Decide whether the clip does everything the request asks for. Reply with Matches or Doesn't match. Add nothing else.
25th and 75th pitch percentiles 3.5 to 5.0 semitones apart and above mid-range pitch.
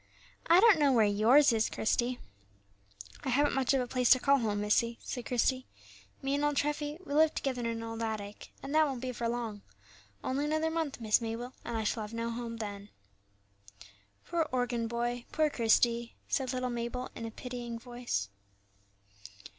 Doesn't match